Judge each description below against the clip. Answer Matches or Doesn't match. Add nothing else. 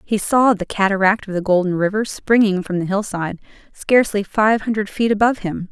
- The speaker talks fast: Doesn't match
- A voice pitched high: Matches